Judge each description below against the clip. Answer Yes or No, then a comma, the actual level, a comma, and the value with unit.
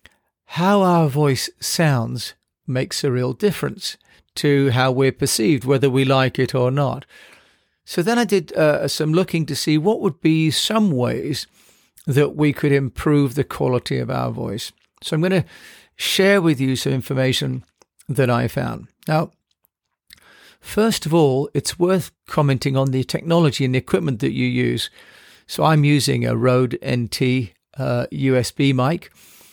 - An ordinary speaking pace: Yes, average, 160 wpm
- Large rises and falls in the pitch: No, average, 3.6 semitones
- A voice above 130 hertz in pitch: Yes, medium, 140 Hz